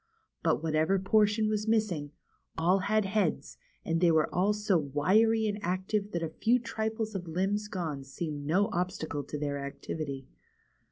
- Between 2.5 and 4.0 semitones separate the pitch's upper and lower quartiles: No, average, 5.1 semitones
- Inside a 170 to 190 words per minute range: No, average, 160 wpm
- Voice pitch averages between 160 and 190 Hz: Yes, medium, 185 Hz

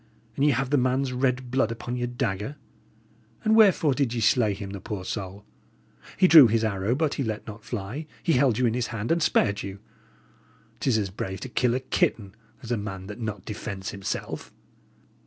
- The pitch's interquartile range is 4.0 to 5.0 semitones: Yes, average, 4.3 semitones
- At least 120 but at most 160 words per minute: No, average, 200 wpm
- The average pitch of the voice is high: No, low, 115 Hz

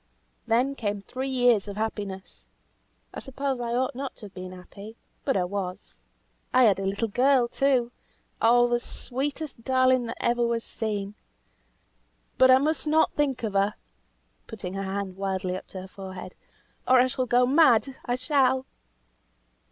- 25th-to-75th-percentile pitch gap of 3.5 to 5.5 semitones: Yes, average, 4.5 semitones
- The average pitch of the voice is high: Yes, high, 235 Hz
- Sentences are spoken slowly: No, average, 165 wpm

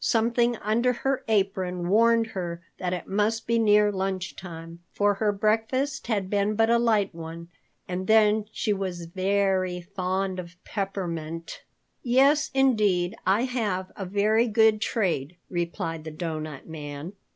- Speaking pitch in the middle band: No, high, 195 Hz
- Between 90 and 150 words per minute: Yes, average, 145 wpm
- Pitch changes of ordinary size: Yes, average, 3.8 semitones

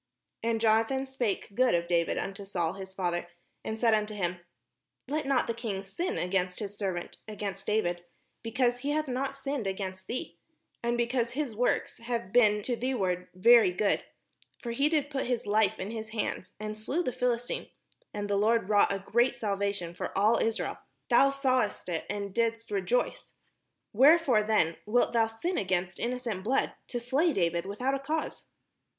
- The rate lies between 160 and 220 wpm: Yes, average, 180 wpm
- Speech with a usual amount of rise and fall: Yes, average, 4.1 semitones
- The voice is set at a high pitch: Yes, high, 220 Hz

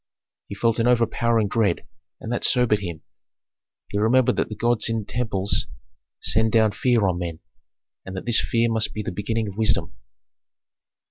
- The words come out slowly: No, average, 170 wpm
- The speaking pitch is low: Yes, low, 110 Hz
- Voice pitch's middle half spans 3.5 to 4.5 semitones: No, narrow, 2.6 semitones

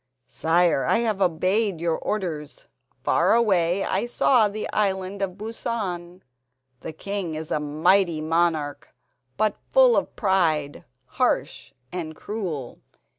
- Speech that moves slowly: Yes, slow, 125 wpm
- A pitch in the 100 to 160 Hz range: No, medium, 185 Hz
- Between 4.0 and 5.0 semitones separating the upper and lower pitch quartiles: Yes, average, 4.3 semitones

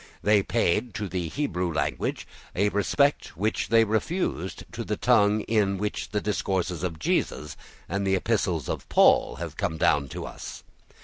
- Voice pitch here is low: Yes, low, 100 Hz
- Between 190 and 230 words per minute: No, average, 165 wpm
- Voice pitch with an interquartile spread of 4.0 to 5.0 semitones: No, average, 3.5 semitones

